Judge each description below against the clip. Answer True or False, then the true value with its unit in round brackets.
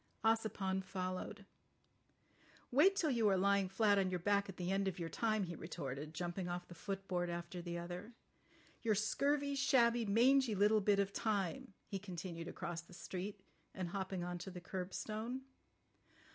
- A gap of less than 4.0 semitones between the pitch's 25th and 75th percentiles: True (3.5 semitones)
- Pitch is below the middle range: False (195 Hz)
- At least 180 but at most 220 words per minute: False (165 wpm)